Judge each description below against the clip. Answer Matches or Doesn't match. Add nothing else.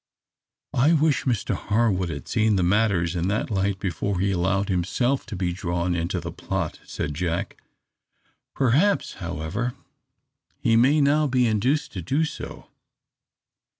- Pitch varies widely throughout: Matches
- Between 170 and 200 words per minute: Doesn't match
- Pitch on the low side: Matches